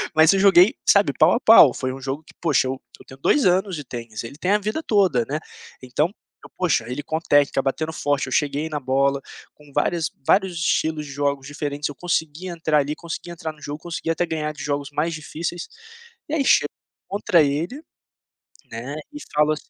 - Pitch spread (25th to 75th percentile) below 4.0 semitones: Yes, average, 3.5 semitones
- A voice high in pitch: No, medium, 150 Hz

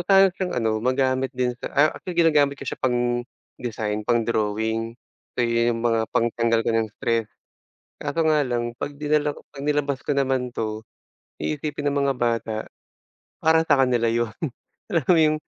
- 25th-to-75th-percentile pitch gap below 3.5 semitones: No, average, 4.1 semitones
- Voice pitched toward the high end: No, low, 125 Hz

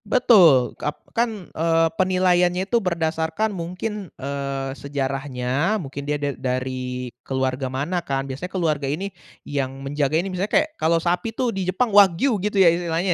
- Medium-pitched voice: Yes, medium, 165 Hz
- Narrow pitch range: No, average, 5.3 semitones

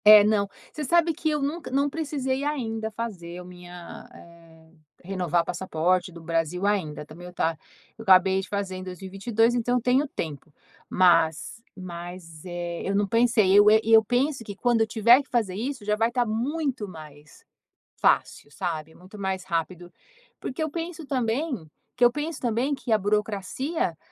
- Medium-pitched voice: No, high, 205 Hz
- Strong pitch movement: Yes, wide, 5.7 semitones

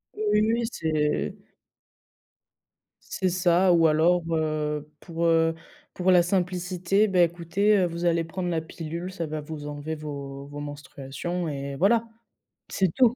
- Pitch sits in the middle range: Yes, medium, 170 Hz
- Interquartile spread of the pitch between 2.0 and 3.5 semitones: Yes, average, 3.2 semitones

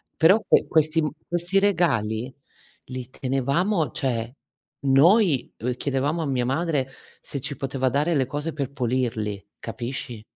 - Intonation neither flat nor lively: Yes, average, 4.4 semitones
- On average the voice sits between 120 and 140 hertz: Yes, low, 135 Hz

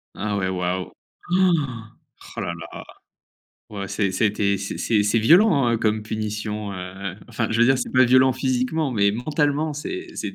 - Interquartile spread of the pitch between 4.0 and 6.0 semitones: Yes, average, 4.6 semitones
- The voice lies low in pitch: Yes, low, 110 Hz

